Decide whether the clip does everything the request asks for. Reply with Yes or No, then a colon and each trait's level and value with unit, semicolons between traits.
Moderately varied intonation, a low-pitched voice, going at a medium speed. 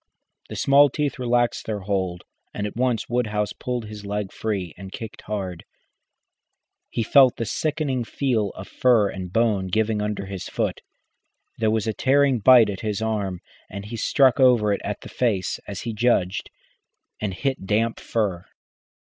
Yes: average, 3.5 semitones; low, 110 Hz; average, 165 wpm